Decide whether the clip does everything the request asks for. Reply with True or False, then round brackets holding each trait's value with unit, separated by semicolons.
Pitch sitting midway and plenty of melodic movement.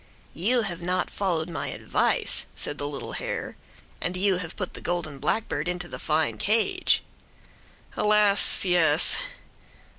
False (180 Hz; 3.8 semitones)